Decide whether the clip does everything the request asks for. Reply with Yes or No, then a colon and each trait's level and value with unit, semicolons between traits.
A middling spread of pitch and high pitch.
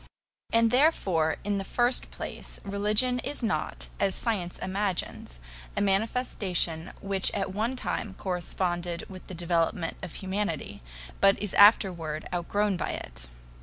Yes: average, 3.3 semitones; high, 195 Hz